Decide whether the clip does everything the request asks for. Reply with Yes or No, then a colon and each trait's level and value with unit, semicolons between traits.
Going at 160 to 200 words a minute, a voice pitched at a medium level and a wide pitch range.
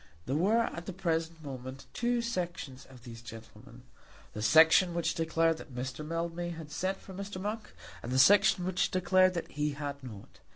Yes: average, 180 wpm; medium, 165 Hz; wide, 5.8 semitones